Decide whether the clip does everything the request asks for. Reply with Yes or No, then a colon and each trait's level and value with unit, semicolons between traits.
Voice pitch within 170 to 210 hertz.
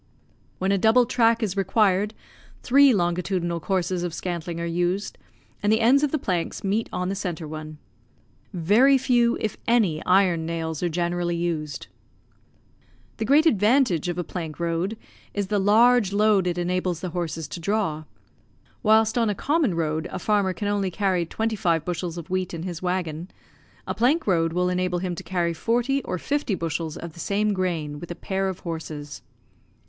Yes: medium, 185 Hz